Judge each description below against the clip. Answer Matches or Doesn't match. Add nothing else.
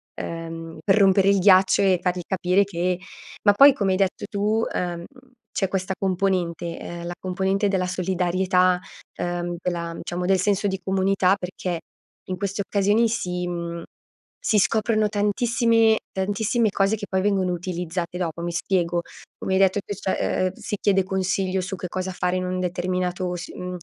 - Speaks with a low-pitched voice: Doesn't match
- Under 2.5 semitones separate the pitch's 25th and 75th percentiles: Matches